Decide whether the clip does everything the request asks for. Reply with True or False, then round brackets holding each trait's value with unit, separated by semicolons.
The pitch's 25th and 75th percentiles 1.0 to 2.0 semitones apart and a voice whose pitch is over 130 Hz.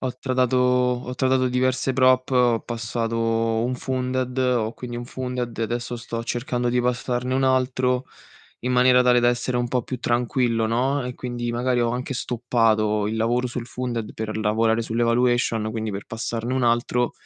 False (1.6 semitones; 120 Hz)